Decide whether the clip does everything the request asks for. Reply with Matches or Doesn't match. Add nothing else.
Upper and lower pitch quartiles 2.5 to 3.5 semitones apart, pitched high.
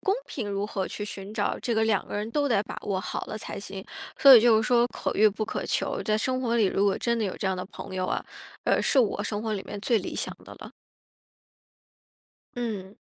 Matches